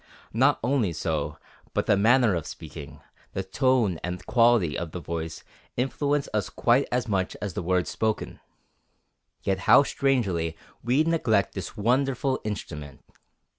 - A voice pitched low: Yes, low, 105 Hz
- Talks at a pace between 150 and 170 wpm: No, average, 140 wpm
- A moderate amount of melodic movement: No, wide, 6.4 semitones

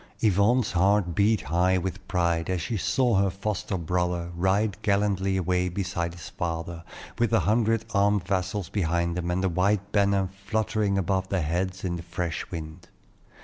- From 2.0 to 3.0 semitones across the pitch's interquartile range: Yes, average, 2.7 semitones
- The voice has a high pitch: No, very low, 95 Hz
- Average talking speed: Yes, average, 165 wpm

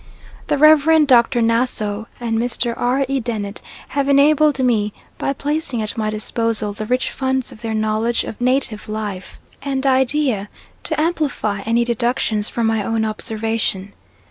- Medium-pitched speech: No, high, 235 Hz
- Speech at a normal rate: Yes, average, 150 wpm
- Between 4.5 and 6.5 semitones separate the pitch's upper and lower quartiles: No, average, 3.8 semitones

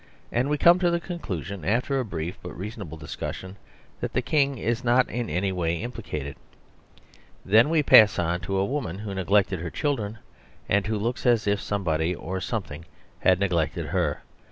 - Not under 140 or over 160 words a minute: No, average, 180 wpm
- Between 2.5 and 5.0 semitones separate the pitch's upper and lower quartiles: No, wide, 5.6 semitones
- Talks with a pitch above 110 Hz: No, low, 100 Hz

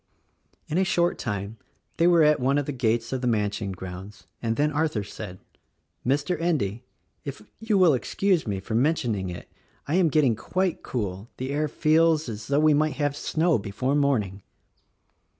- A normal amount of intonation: No, wide, 6.7 semitones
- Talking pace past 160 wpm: Yes, average, 185 wpm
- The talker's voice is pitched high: No, low, 135 Hz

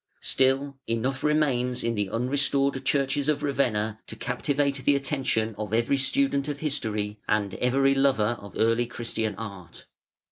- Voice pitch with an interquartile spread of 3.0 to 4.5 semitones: Yes, average, 3.8 semitones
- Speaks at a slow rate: No, average, 150 wpm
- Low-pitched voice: Yes, low, 130 Hz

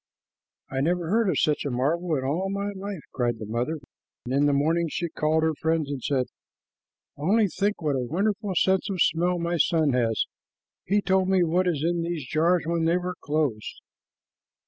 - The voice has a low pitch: No, medium, 165 Hz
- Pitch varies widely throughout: No, average, 4.0 semitones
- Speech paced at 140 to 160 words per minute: No, average, 190 wpm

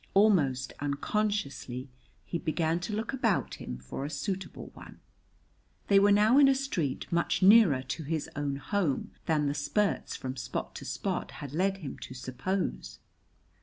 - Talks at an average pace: Yes, average, 160 wpm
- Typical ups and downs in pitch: No, wide, 6.6 semitones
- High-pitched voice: No, medium, 165 Hz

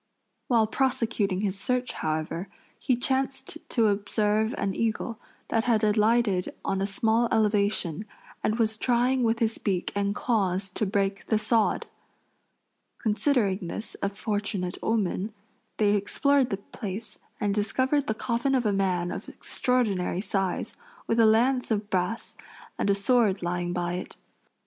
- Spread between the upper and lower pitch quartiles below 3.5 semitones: Yes, average, 3.0 semitones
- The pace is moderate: Yes, average, 145 wpm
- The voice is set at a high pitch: Yes, high, 215 Hz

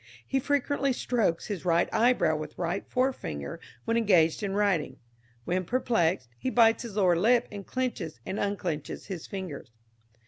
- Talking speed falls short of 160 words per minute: Yes, average, 150 wpm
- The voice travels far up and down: Yes, wide, 6.1 semitones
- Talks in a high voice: Yes, high, 200 Hz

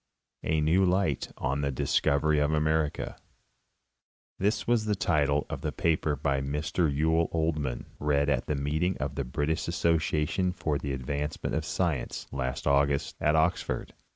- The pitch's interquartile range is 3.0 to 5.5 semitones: No, narrow, 2.6 semitones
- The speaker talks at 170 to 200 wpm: No, average, 155 wpm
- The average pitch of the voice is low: Yes, very low, 75 Hz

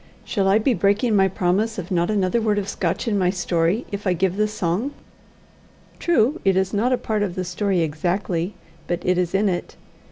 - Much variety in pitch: No, average, 2.9 semitones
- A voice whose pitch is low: No, high, 195 Hz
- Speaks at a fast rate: Yes, fast, 210 wpm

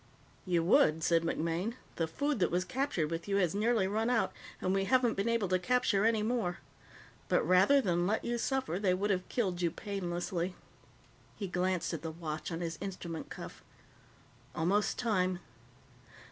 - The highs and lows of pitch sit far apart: No, average, 4.2 semitones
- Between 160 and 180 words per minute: Yes, average, 175 wpm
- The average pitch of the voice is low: No, medium, 185 Hz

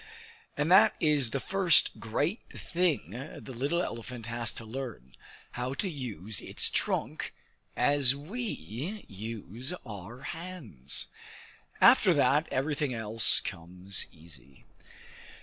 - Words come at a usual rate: No, slow, 115 wpm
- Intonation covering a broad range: Yes, wide, 5.9 semitones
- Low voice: Yes, low, 125 Hz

